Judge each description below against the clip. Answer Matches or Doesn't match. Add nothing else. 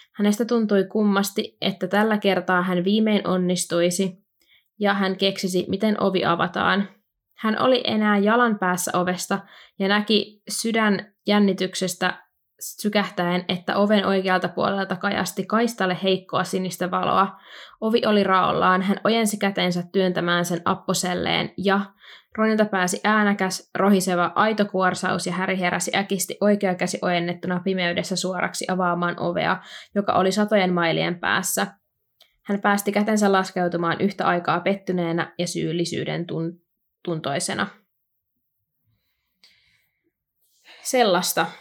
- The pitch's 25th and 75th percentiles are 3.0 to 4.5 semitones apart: Doesn't match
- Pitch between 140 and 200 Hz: Matches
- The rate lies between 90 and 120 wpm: Matches